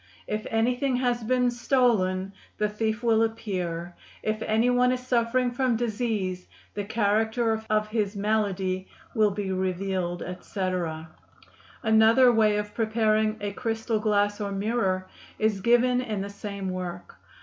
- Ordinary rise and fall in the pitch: Yes, average, 3.1 semitones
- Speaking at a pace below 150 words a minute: Yes, average, 140 wpm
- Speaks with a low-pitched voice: No, high, 215 Hz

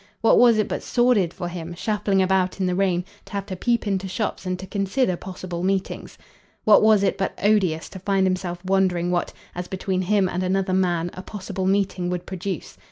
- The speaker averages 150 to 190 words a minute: No, fast, 205 wpm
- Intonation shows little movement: Yes, narrow, 1.7 semitones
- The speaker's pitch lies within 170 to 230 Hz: Yes, high, 190 Hz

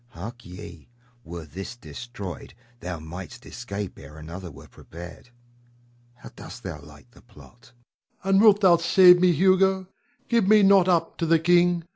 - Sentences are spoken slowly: No, average, 160 wpm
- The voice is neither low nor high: No, low, 125 Hz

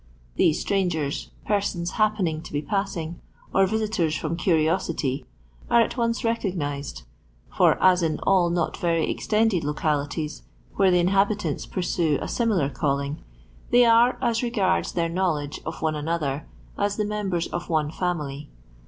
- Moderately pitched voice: Yes, medium, 175 Hz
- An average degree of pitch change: Yes, average, 4.8 semitones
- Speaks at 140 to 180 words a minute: Yes, average, 150 wpm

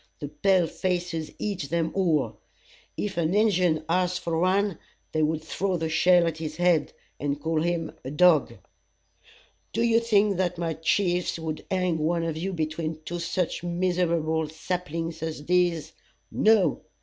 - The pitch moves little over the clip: Yes, narrow, 2.3 semitones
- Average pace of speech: Yes, average, 155 wpm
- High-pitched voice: No, medium, 170 Hz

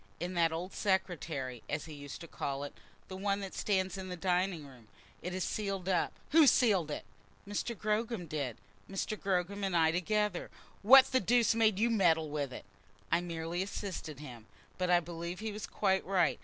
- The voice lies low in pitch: No, medium, 180 Hz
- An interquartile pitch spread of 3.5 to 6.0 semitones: Yes, average, 3.8 semitones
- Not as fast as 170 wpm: No, average, 190 wpm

